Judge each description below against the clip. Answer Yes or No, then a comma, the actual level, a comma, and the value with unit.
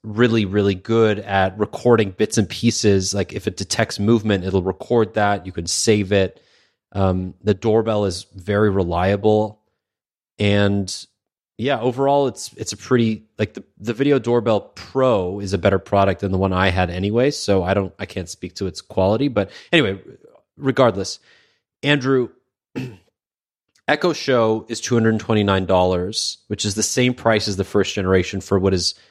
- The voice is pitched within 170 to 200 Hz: No, low, 105 Hz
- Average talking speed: Yes, average, 170 wpm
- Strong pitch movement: No, average, 2.7 semitones